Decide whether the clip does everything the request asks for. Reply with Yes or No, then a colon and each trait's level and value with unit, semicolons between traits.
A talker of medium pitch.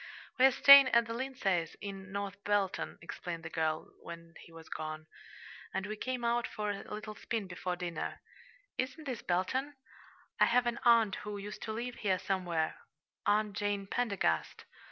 No: high, 205 Hz